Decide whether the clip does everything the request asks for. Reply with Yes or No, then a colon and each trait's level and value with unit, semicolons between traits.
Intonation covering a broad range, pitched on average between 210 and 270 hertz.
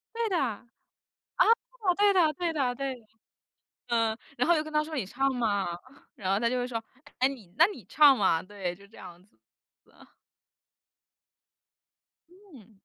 Yes: wide, 7.0 semitones; high, 245 Hz